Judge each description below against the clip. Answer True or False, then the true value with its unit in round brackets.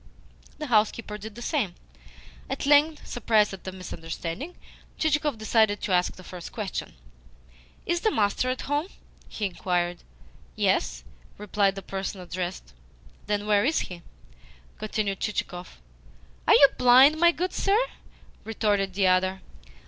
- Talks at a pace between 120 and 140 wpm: True (135 wpm)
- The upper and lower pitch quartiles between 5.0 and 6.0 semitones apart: True (5.6 semitones)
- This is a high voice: True (210 Hz)